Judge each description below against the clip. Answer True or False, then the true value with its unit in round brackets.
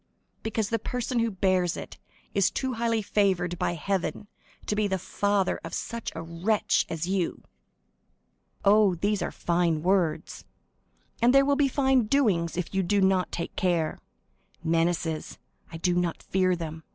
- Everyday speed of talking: True (155 wpm)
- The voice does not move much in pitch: False (3.9 semitones)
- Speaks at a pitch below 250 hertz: True (190 Hz)